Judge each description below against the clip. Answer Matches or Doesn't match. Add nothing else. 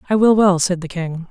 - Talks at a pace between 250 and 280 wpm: Matches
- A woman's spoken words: Matches